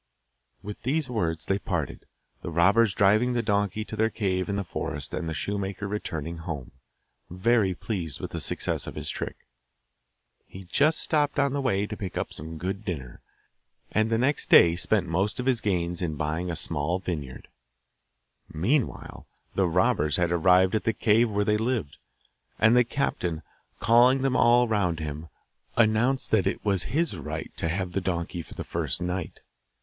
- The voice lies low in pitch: Yes, very low, 95 Hz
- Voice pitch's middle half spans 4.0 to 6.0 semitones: Yes, average, 4.9 semitones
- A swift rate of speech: No, average, 175 wpm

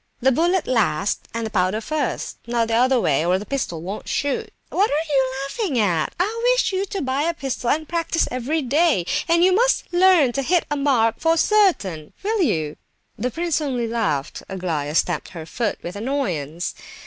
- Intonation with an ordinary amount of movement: No, wide, 8.9 semitones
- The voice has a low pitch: No, very high, 260 Hz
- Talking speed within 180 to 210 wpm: Yes, average, 190 wpm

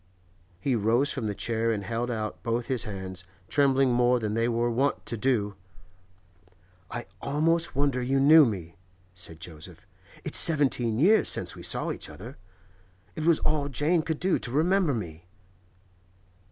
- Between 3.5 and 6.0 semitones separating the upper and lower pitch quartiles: Yes, average, 5.0 semitones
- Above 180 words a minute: No, average, 160 wpm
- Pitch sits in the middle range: No, low, 120 Hz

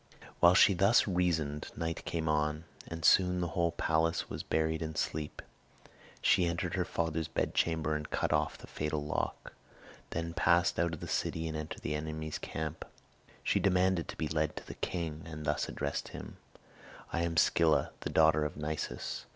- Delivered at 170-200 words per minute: Yes, average, 175 wpm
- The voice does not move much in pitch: Yes, narrow, 1.6 semitones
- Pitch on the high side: No, very low, 80 Hz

